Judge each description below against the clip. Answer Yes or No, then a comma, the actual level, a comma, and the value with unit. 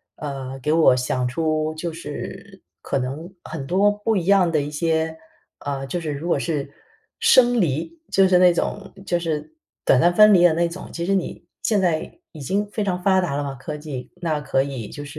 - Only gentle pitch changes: No, average, 4.0 semitones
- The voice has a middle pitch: Yes, medium, 160 Hz